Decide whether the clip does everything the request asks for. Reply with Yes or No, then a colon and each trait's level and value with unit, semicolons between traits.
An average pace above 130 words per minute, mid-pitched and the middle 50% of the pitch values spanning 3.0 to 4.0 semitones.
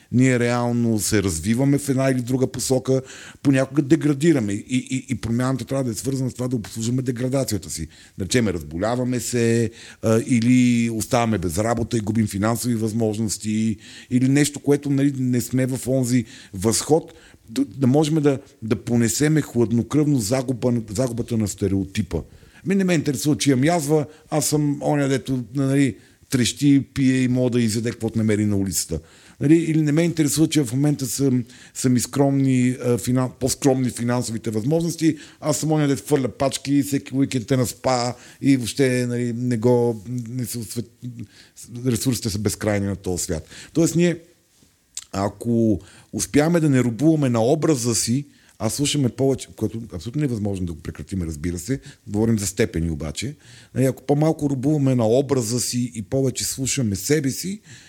No: average, 160 wpm; low, 125 Hz; average, 3.6 semitones